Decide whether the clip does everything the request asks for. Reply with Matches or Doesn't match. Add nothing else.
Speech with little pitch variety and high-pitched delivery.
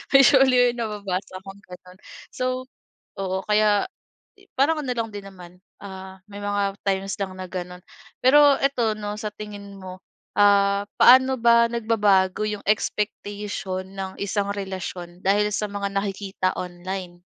Matches